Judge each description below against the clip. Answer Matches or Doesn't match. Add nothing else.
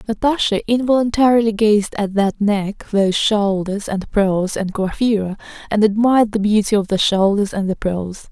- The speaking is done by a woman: Matches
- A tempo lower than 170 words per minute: Matches